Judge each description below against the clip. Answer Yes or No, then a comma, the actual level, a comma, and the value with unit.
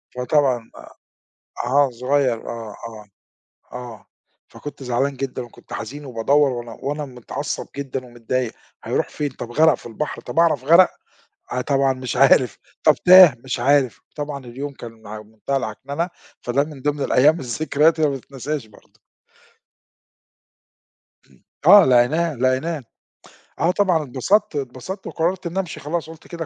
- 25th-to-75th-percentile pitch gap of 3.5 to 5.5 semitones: Yes, average, 3.8 semitones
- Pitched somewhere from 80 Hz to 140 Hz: Yes, low, 135 Hz